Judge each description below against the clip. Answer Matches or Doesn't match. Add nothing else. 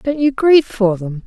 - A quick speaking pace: Matches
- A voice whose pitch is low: Doesn't match